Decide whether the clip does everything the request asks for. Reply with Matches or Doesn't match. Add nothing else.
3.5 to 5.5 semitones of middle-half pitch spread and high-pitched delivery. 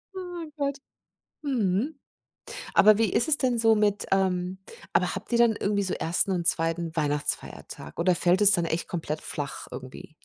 Matches